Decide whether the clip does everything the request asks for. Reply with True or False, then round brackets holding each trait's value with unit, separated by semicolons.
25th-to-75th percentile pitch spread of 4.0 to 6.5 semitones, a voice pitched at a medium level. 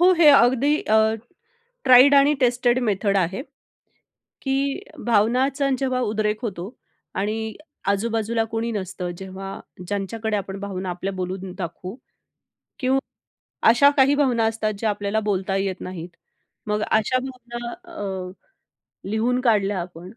False (4.3 semitones; 220 Hz)